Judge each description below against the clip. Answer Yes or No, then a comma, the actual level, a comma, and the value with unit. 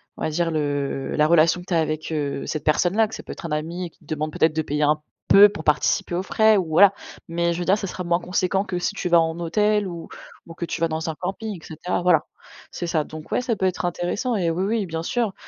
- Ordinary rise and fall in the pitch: Yes, average, 3.1 semitones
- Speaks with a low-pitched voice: No, medium, 170 Hz